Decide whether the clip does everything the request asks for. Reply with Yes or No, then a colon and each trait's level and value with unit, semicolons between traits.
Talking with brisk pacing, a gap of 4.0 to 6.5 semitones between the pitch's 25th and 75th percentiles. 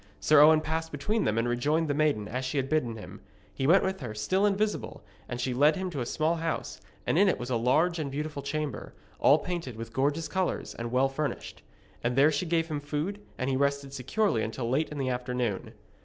Yes: fast, 225 wpm; average, 4.3 semitones